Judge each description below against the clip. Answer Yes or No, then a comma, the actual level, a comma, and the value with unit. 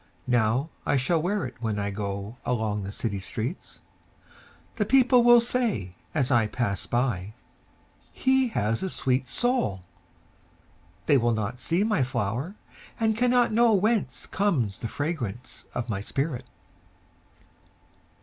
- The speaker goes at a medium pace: No, slow, 110 wpm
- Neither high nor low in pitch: No, low, 125 Hz